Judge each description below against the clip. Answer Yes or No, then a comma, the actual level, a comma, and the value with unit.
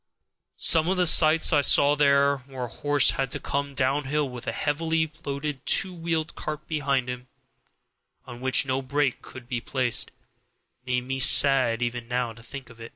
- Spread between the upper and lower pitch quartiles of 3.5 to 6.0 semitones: No, average, 2.8 semitones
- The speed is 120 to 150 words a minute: No, average, 175 wpm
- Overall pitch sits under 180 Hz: Yes, low, 135 Hz